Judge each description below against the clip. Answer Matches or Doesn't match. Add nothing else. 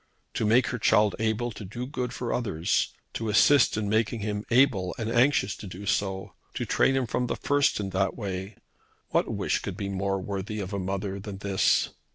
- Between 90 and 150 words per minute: Doesn't match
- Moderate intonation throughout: Matches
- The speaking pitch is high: Doesn't match